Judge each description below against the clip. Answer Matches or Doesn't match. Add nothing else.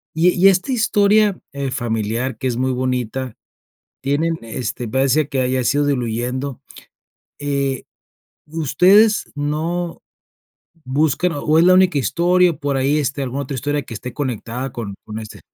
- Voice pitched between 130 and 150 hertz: Matches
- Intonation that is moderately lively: Matches